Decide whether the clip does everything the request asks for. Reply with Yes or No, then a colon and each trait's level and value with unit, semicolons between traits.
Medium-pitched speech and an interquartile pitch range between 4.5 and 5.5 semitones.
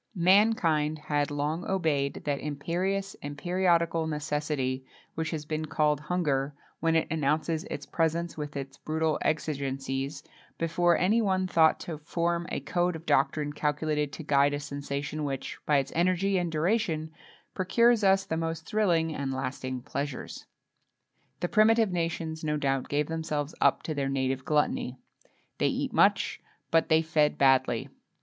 No: medium, 155 Hz; average, 3.0 semitones